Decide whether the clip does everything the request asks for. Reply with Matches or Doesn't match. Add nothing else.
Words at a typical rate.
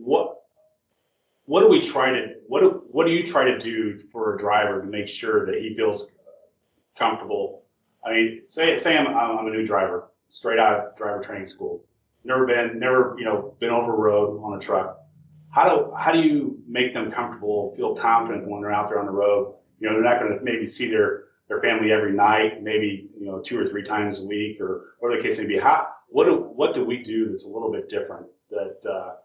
Doesn't match